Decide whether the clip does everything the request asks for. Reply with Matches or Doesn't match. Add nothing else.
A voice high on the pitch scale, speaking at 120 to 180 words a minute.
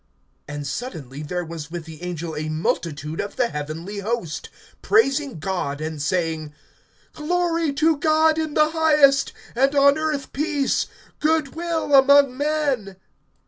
Matches